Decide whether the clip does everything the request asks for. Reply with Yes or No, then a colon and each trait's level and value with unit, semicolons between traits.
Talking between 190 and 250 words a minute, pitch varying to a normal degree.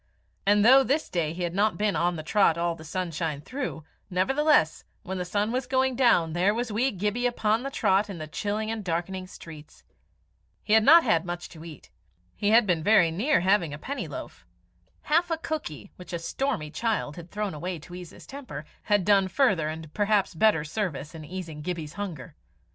Yes: average, 200 wpm; average, 5.0 semitones